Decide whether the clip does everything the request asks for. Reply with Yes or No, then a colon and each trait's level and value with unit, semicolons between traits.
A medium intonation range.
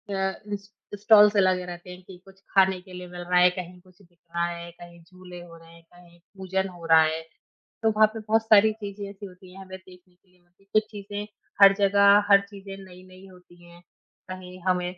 No: narrow, 2.0 semitones